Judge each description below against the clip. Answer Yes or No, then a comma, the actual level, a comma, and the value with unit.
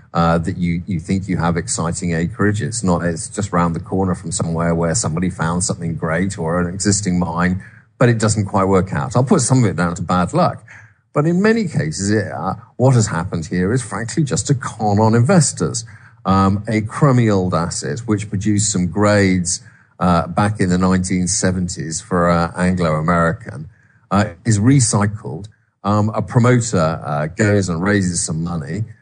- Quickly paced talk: No, average, 185 wpm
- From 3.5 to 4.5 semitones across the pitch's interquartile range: Yes, average, 4.2 semitones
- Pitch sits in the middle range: No, low, 100 Hz